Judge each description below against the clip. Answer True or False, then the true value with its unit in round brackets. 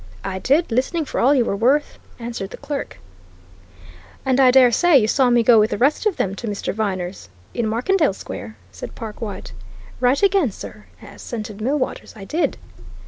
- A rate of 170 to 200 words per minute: True (180 wpm)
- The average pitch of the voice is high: True (240 Hz)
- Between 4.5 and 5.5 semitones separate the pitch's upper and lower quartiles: True (4.8 semitones)